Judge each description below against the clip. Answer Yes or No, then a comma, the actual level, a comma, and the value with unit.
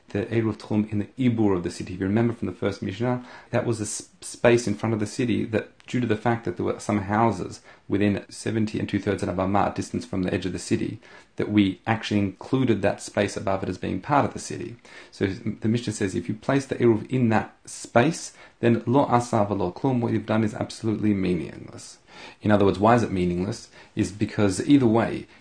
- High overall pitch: No, low, 105 Hz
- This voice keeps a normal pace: No, fast, 230 wpm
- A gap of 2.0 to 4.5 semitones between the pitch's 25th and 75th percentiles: Yes, narrow, 2.6 semitones